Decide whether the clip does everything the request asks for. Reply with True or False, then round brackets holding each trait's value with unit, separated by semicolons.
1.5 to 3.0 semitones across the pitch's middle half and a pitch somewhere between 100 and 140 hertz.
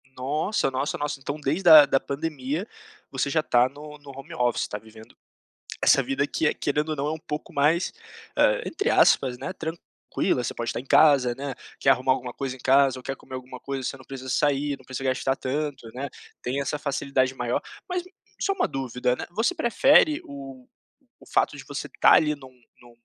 True (2.7 semitones; 135 Hz)